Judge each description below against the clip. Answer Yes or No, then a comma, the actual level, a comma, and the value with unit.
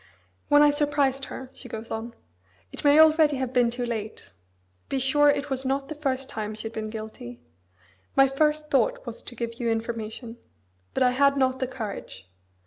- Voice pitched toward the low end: No, very high, 260 Hz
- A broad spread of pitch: No, average, 3.9 semitones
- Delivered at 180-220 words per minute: Yes, average, 190 wpm